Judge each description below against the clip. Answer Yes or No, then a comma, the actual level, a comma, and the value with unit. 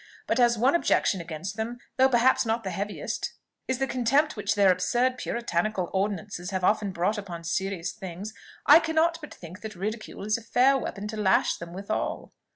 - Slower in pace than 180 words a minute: No, average, 185 wpm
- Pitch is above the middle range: Yes, high, 210 Hz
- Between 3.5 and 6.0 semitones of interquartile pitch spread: Yes, average, 4.2 semitones